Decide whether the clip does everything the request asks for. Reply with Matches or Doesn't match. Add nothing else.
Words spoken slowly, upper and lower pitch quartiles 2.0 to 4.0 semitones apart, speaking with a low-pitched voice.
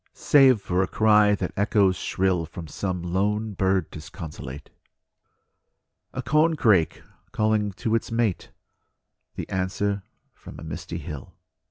Matches